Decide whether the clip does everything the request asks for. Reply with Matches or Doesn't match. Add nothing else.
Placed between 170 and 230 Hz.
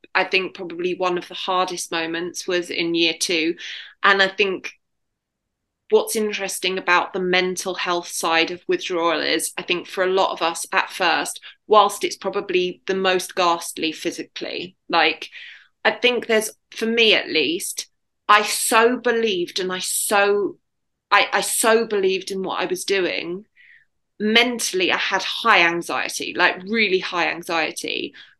Matches